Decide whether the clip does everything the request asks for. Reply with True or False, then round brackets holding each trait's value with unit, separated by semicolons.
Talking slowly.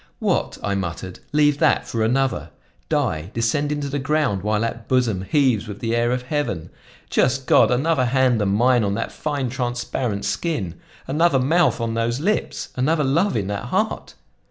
False (175 wpm)